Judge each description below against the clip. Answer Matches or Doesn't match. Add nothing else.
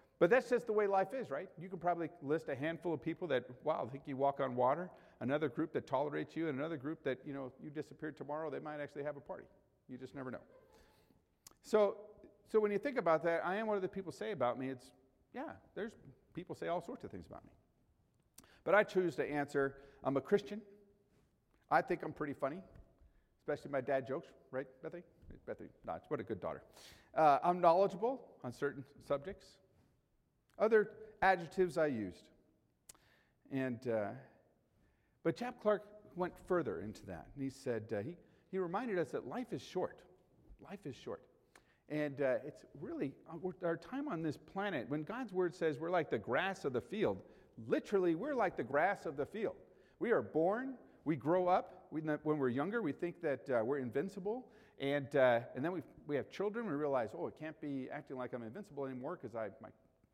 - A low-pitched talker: Doesn't match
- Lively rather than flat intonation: Matches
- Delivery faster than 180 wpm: Matches